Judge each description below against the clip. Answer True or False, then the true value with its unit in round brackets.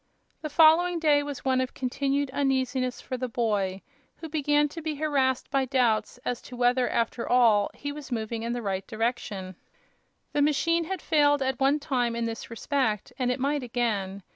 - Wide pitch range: False (3.7 semitones)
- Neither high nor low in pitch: False (260 Hz)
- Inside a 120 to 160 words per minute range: False (185 wpm)